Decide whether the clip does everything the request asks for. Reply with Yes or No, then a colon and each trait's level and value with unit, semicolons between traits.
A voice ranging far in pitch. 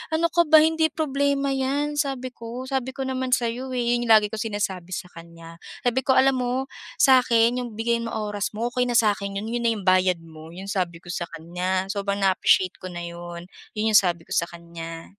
Yes: wide, 6.3 semitones